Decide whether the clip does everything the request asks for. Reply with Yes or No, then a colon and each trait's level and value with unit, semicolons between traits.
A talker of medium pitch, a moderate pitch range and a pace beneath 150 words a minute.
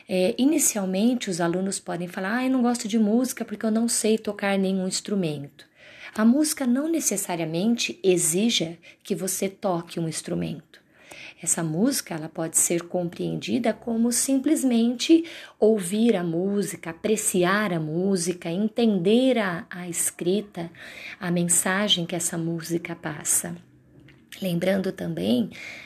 No: high, 195 Hz; average, 4.8 semitones; average, 130 wpm